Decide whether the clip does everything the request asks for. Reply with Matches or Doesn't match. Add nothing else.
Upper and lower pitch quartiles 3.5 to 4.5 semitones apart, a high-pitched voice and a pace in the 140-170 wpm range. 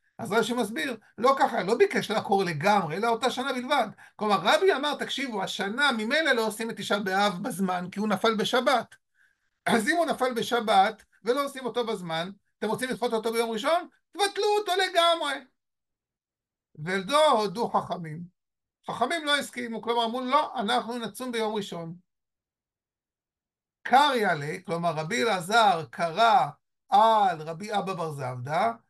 Doesn't match